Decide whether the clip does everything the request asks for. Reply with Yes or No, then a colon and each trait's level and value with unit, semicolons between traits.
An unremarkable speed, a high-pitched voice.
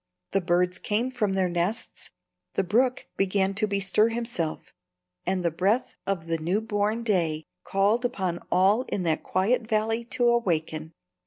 Yes: average, 155 wpm; high, 195 Hz